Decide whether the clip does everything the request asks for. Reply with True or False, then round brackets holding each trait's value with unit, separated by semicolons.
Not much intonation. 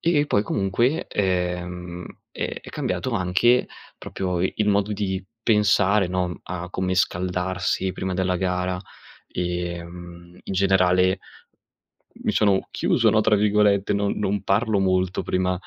True (2.2 semitones)